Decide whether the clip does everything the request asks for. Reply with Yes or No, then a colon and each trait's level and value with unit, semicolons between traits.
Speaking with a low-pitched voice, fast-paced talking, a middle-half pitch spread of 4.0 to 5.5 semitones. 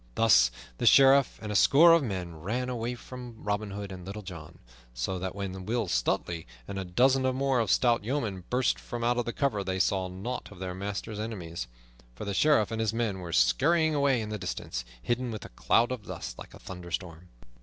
Yes: low, 105 Hz; fast, 215 wpm; average, 5.0 semitones